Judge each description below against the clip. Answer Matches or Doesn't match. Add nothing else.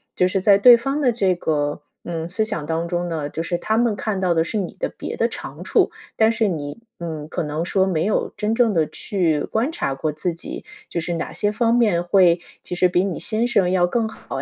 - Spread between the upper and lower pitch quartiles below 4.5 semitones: Doesn't match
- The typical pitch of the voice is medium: Matches